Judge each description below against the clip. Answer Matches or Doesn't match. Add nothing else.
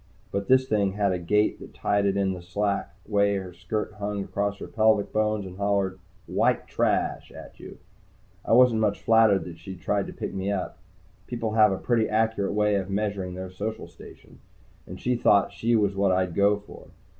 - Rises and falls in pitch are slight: Matches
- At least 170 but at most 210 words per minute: Matches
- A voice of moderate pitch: Doesn't match